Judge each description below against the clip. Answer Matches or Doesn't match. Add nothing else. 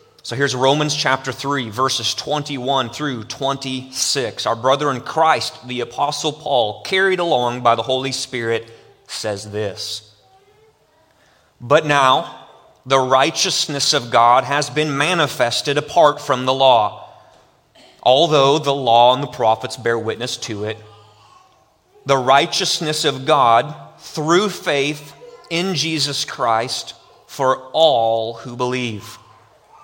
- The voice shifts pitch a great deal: Doesn't match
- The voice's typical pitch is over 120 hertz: Matches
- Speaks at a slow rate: Matches